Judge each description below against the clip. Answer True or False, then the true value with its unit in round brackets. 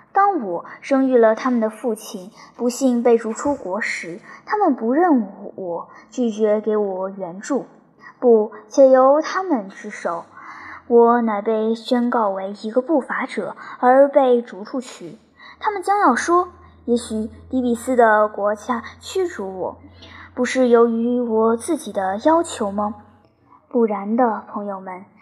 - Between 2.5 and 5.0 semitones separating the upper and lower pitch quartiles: True (3.8 semitones)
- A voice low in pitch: False (235 Hz)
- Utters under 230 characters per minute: True (200 characters per minute)